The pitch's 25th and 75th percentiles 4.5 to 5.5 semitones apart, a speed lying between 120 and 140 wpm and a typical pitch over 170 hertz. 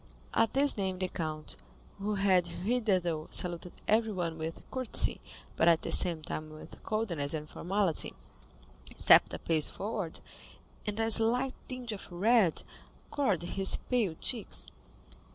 Yes: average, 5.2 semitones; slow, 135 wpm; high, 190 Hz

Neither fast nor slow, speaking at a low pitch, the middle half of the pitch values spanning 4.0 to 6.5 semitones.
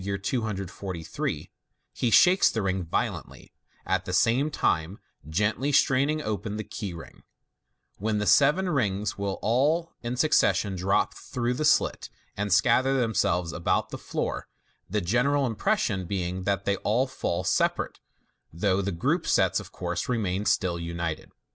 Yes: average, 145 wpm; low, 105 Hz; average, 5.2 semitones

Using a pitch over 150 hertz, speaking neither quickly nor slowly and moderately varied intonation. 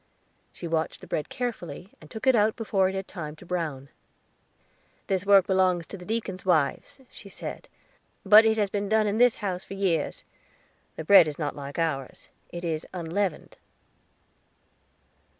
Yes: medium, 185 Hz; average, 170 wpm; average, 4.0 semitones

